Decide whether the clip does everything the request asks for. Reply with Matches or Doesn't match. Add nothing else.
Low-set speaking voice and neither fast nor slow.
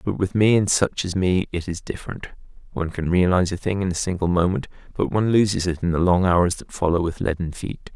Doesn't match